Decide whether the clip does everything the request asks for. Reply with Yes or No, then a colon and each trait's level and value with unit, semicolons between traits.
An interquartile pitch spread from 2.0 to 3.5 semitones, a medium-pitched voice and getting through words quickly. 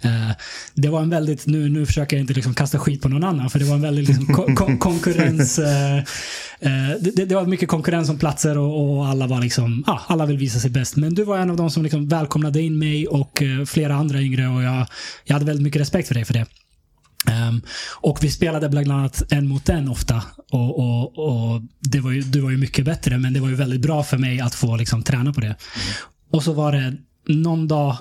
Yes: average, 2.7 semitones; medium, 145 Hz; fast, 245 wpm